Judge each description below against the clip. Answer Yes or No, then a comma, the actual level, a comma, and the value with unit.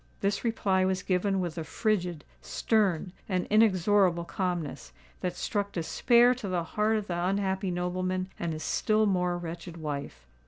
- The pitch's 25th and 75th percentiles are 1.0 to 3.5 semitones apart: Yes, average, 2.8 semitones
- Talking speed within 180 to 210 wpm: No, average, 145 wpm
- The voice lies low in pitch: No, medium, 185 Hz